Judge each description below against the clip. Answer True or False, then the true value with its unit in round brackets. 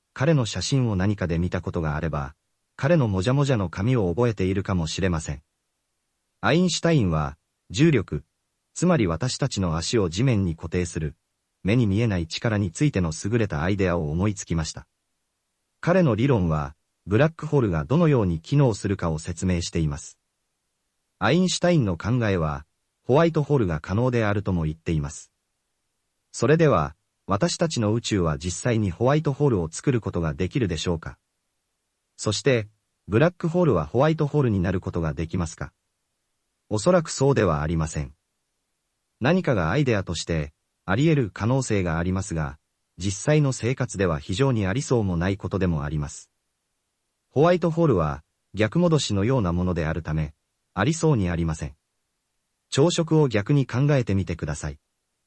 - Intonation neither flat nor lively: False (7.7 semitones)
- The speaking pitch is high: False (100 Hz)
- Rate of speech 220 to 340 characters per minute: False (355 characters per minute)